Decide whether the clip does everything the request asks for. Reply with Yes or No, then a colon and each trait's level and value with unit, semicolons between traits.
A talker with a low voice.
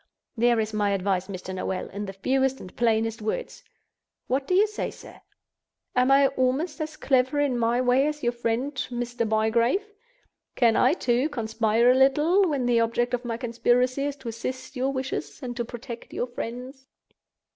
No: high, 245 Hz